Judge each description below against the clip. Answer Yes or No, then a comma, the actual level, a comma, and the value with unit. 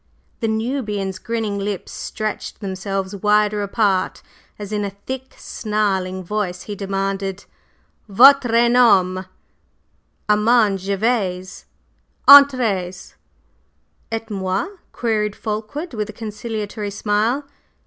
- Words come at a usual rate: No, slow, 95 wpm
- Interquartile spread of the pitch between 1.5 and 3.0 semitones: Yes, narrow, 2.5 semitones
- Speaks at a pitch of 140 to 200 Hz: No, high, 210 Hz